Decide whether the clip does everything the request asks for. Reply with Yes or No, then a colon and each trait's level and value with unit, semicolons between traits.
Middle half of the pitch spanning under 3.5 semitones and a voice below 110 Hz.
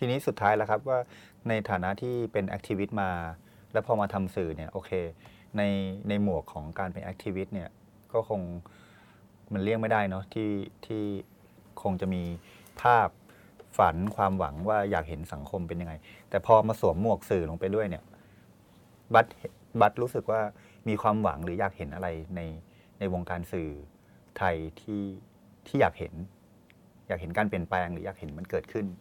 Yes: average, 2.9 semitones; low, 100 Hz